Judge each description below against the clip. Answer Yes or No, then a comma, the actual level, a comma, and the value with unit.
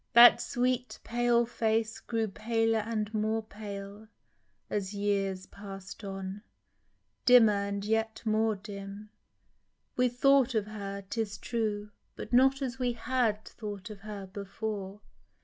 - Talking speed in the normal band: No, slow, 130 wpm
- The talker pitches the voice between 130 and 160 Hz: No, high, 215 Hz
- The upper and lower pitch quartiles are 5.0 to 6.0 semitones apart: No, narrow, 2.4 semitones